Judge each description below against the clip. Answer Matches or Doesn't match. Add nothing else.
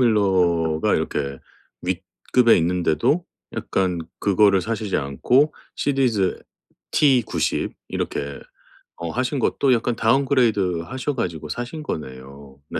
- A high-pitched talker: Doesn't match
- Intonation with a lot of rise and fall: Matches